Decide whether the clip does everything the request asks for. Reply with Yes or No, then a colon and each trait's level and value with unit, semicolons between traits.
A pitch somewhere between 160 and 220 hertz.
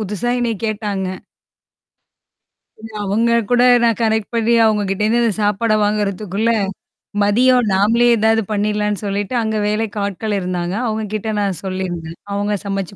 Yes: high, 210 Hz